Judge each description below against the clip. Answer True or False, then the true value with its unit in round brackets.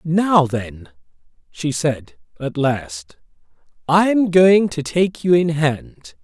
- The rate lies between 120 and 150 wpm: True (135 wpm)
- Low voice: False (150 Hz)